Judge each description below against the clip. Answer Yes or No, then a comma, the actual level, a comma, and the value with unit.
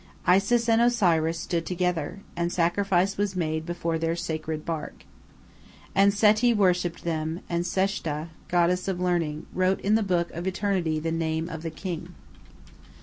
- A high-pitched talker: No, medium, 175 Hz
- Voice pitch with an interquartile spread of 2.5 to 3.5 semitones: Yes, average, 3.0 semitones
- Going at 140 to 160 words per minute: Yes, average, 150 wpm